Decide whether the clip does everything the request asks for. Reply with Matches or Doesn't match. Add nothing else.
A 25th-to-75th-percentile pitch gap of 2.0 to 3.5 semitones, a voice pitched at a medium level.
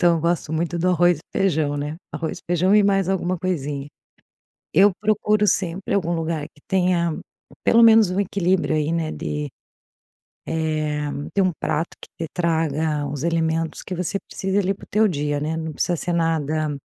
Matches